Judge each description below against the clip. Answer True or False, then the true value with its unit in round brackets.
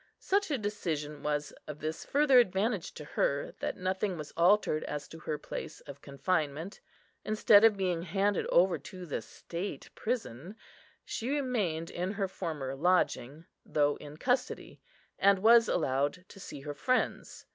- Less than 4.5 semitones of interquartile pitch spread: False (5.6 semitones)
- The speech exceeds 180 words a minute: False (155 wpm)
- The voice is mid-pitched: True (180 Hz)